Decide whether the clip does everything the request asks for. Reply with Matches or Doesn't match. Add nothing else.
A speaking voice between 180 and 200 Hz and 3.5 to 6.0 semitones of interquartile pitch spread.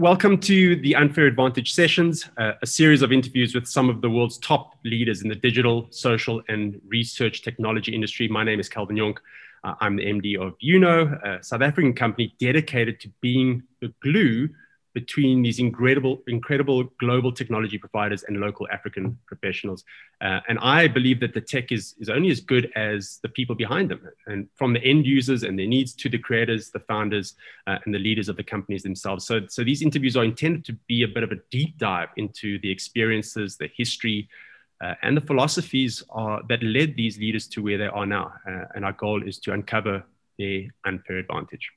Doesn't match